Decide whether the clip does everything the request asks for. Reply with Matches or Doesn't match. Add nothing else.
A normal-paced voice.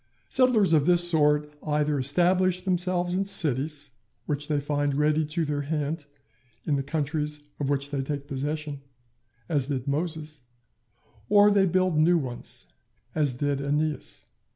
Matches